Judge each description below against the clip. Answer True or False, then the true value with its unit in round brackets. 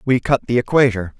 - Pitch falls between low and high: False (120 Hz)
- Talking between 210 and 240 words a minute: False (200 wpm)